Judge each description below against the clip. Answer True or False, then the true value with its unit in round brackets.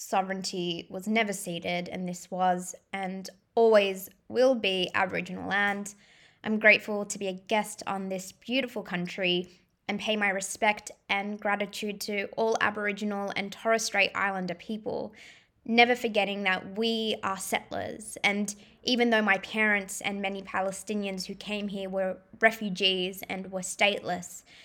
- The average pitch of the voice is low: False (200 Hz)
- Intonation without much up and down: True (2.1 semitones)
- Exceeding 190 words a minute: False (145 wpm)